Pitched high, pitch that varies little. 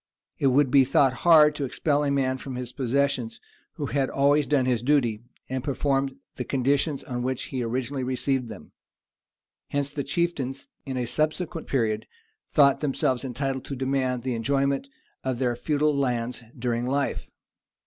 No: low, 135 Hz; narrow, 2.1 semitones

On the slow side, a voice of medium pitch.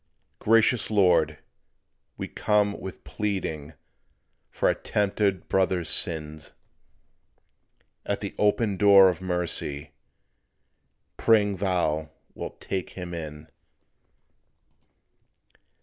No: slow, 85 wpm; very low, 95 Hz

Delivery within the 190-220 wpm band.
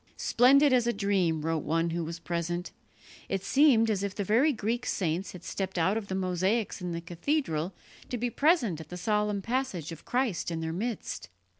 Yes: average, 195 wpm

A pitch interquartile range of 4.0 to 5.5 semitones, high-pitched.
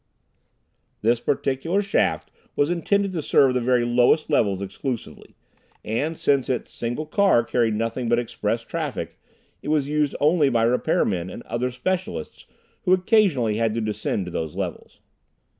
No: average, 5.2 semitones; low, 125 Hz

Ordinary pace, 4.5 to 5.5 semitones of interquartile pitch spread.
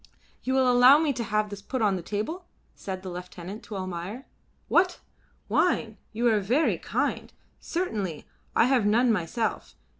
Yes: average, 160 wpm; average, 4.9 semitones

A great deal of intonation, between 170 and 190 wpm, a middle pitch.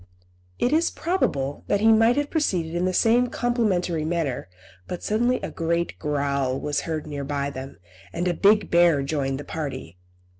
Yes: wide, 7.5 semitones; average, 175 wpm; medium, 170 Hz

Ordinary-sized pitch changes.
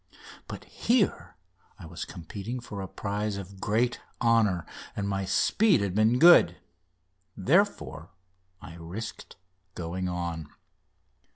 Yes: average, 4.5 semitones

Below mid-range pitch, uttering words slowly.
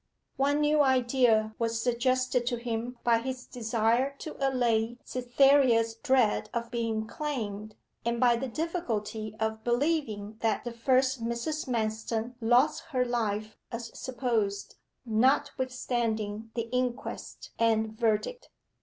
No: high, 235 Hz; slow, 120 wpm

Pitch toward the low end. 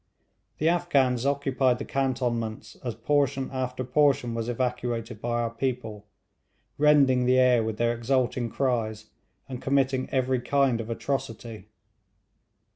Yes: low, 125 Hz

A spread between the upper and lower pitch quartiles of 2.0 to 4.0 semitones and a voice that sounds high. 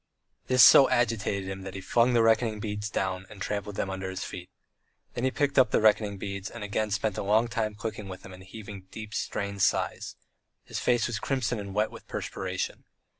No: average, 2.8 semitones; low, 105 Hz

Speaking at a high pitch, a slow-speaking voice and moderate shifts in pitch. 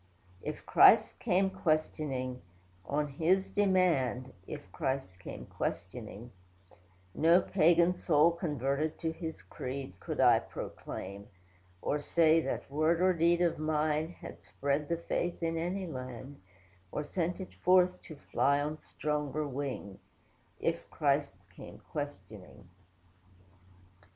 No: medium, 150 Hz; slow, 120 wpm; average, 4.3 semitones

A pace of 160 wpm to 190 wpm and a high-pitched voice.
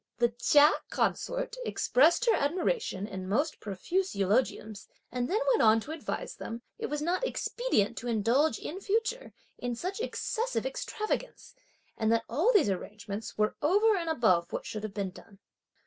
Yes: average, 165 wpm; very high, 280 Hz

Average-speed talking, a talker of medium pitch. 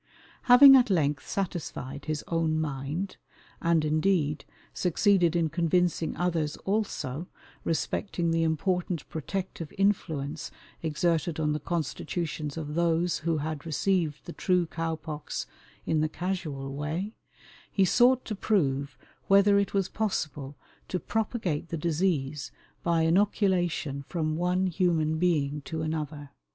No: slow, 125 wpm; medium, 165 Hz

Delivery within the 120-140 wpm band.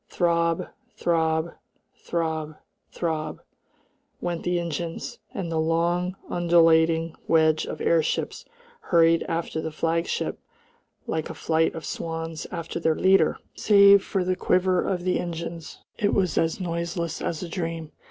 Yes: slow, 135 wpm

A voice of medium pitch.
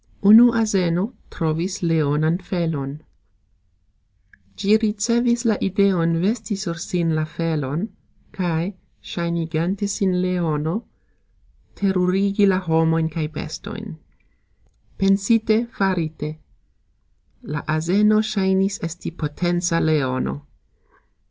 Yes: medium, 180 Hz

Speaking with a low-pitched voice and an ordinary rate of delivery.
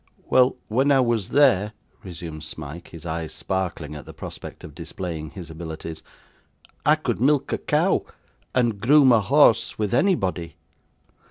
Yes: very low, 95 Hz; average, 150 wpm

